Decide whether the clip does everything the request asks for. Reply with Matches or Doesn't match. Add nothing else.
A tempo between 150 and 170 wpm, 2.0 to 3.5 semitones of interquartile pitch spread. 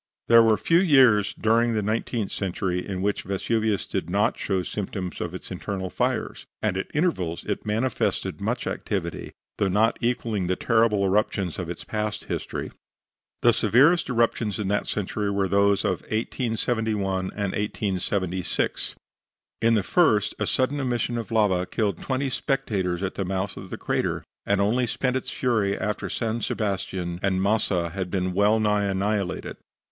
Matches